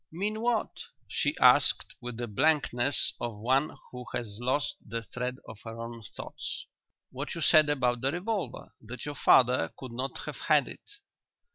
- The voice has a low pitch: Yes, low, 125 Hz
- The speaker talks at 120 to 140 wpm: No, average, 165 wpm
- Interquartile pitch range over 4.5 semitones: No, average, 4.2 semitones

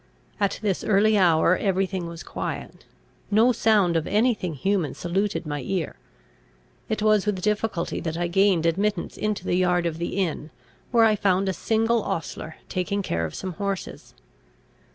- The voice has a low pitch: No, high, 190 Hz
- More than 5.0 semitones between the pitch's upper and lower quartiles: No, average, 3.5 semitones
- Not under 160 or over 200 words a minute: Yes, average, 170 wpm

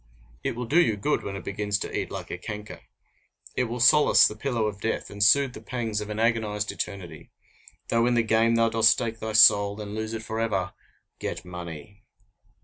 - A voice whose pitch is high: No, low, 110 Hz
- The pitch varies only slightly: Yes, narrow, 2.0 semitones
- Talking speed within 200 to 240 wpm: Yes, fast, 205 wpm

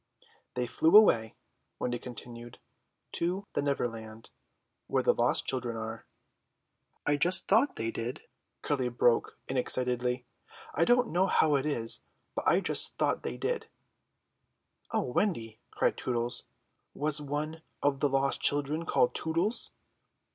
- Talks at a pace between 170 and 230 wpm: No, slow, 135 wpm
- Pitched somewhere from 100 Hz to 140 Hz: Yes, low, 135 Hz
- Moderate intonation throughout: Yes, average, 4.8 semitones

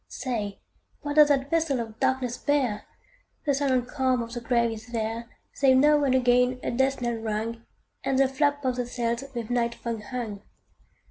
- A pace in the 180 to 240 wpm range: Yes, average, 185 wpm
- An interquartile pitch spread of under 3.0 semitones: Yes, narrow, 2.5 semitones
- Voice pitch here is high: Yes, very high, 250 Hz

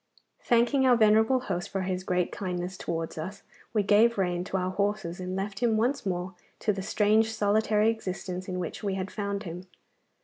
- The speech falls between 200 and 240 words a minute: No, average, 190 wpm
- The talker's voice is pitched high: Yes, high, 200 Hz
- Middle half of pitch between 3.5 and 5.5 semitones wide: No, average, 3.0 semitones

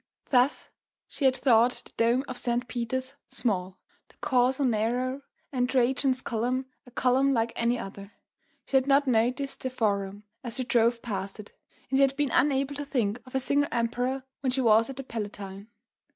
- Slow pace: No, average, 180 wpm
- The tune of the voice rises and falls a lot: No, narrow, 2.6 semitones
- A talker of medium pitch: No, very high, 250 Hz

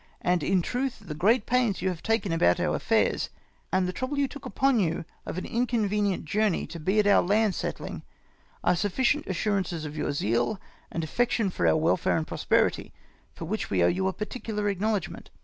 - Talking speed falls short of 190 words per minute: No, average, 195 wpm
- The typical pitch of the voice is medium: No, high, 195 Hz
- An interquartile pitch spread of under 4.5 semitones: No, average, 4.8 semitones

